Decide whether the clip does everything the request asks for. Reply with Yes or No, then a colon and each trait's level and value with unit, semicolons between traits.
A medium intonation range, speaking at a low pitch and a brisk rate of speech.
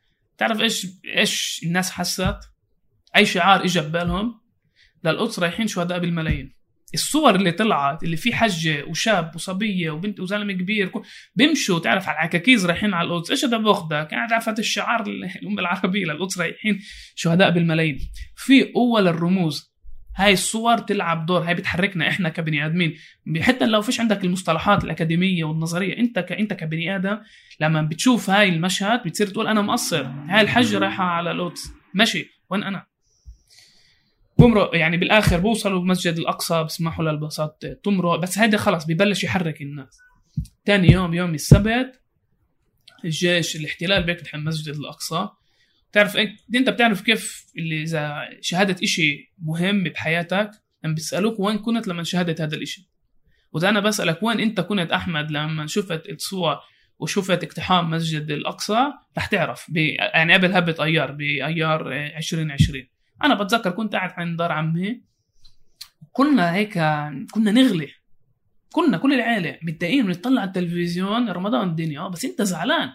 No: average, 4.7 semitones; medium, 180 Hz; fast, 140 wpm